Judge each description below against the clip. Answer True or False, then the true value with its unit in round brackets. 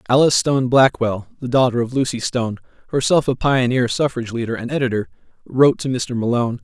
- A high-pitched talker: False (125 Hz)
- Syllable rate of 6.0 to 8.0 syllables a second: True (6.4 syllables/s)